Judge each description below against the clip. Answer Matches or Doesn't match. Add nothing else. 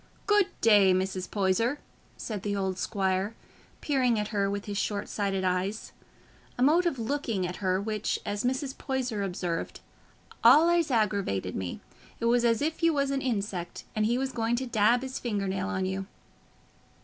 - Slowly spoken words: Doesn't match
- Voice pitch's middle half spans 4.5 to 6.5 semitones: Matches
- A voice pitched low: Doesn't match